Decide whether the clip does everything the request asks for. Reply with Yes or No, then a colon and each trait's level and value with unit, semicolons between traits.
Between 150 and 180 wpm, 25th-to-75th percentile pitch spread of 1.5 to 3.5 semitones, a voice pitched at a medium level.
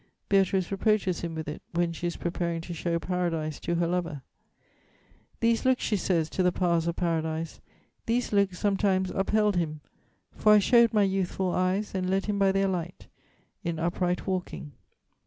Yes: average, 175 wpm; narrow, 2.6 semitones; medium, 180 Hz